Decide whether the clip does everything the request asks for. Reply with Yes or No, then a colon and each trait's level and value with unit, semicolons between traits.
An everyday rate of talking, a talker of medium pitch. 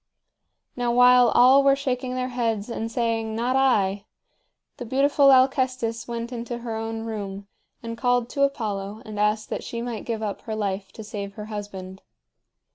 No: average, 170 wpm; high, 230 Hz